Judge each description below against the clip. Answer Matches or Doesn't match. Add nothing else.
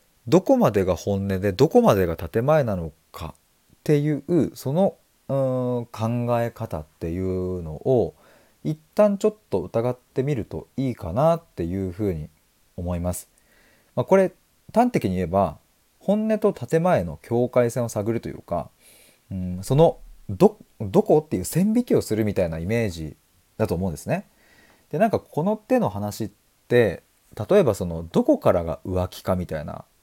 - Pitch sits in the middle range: Doesn't match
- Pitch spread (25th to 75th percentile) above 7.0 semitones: Matches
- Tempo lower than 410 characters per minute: Matches